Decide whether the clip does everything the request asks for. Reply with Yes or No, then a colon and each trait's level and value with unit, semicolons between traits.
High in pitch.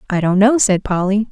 Yes: high, 200 Hz